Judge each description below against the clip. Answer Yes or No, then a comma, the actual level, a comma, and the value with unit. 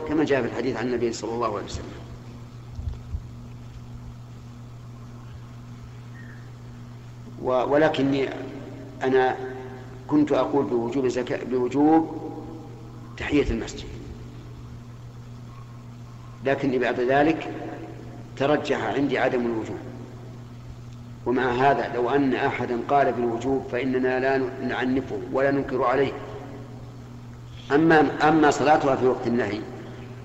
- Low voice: Yes, low, 125 Hz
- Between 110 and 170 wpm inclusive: No, average, 90 wpm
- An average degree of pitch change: No, narrow, 1.9 semitones